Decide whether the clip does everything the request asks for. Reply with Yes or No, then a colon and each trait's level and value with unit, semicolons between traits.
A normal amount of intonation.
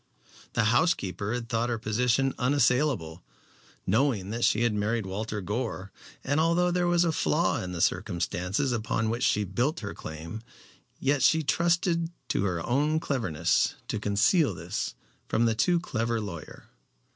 No: wide, 6.2 semitones